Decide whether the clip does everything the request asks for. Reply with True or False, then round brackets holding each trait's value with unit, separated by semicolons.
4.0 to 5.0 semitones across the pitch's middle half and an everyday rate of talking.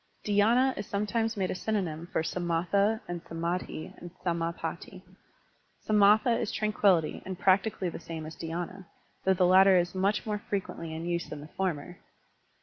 False (3.3 semitones; 155 wpm)